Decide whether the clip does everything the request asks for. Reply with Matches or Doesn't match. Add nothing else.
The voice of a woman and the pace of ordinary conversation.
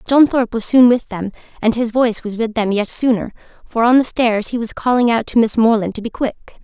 Doesn't match